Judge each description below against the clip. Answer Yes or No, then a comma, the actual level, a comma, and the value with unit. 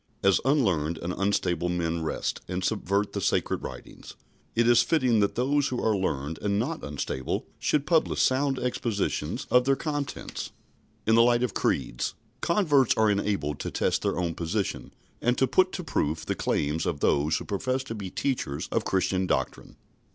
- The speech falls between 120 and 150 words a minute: No, average, 175 wpm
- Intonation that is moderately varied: No, wide, 7.2 semitones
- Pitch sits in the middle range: No, low, 105 Hz